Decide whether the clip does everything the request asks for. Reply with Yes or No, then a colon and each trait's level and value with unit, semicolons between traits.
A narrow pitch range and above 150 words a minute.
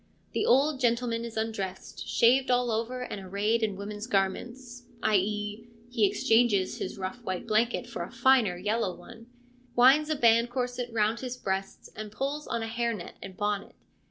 No: average, 3.0 semitones; average, 170 wpm